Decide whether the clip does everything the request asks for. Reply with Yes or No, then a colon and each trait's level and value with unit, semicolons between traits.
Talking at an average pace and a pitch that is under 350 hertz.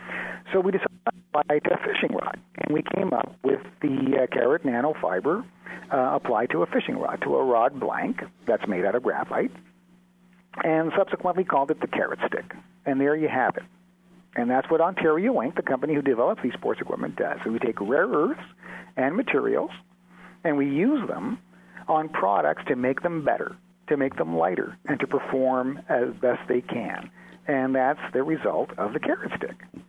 Yes: average, 190 wpm; low, 135 Hz